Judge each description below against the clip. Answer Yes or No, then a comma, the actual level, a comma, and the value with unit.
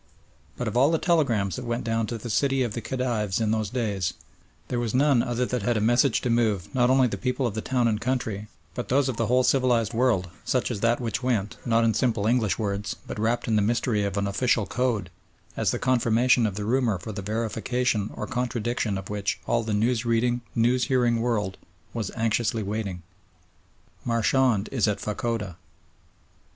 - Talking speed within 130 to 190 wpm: No, average, 200 wpm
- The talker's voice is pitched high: No, low, 115 Hz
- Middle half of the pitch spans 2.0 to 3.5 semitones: Yes, average, 2.9 semitones